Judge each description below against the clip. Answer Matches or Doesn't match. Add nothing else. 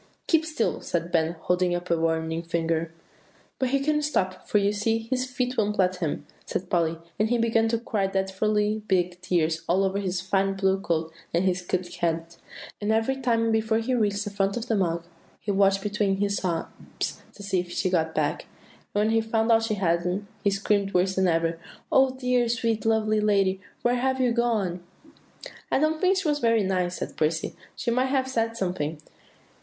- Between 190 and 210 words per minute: Matches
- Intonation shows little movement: Doesn't match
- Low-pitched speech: Doesn't match